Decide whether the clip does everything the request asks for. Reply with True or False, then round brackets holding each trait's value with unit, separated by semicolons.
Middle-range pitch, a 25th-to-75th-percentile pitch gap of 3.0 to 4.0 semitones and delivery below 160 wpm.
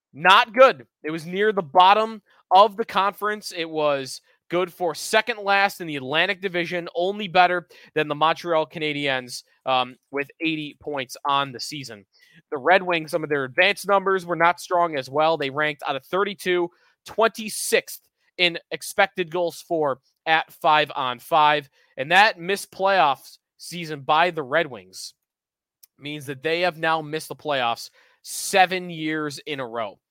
False (165 Hz; 3.7 semitones; 165 wpm)